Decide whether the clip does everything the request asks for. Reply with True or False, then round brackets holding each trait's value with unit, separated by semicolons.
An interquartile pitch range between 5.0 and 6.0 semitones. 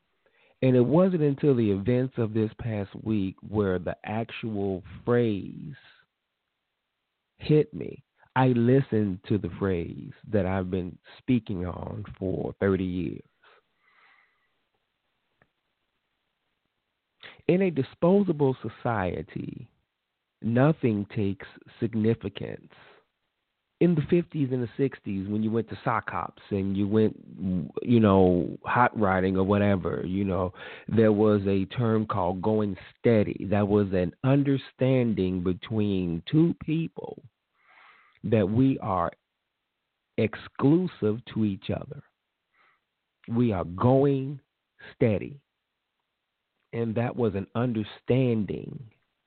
False (4.4 semitones)